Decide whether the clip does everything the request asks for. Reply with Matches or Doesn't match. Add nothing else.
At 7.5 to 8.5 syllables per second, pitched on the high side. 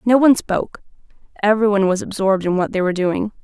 Matches